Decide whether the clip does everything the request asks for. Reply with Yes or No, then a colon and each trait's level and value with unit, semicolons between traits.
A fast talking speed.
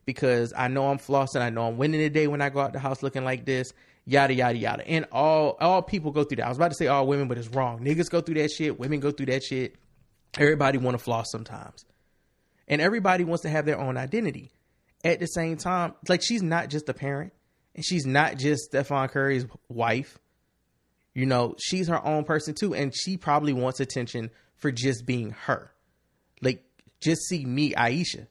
Yes: fast, 215 wpm